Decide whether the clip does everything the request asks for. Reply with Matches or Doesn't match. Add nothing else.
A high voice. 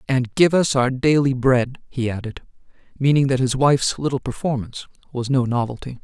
Doesn't match